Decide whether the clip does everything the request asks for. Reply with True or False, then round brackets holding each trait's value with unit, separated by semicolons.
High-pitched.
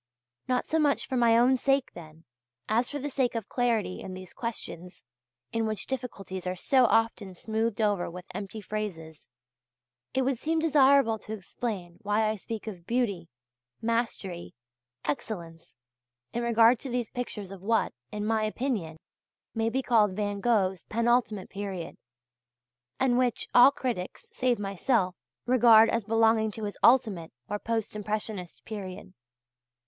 True (220 Hz)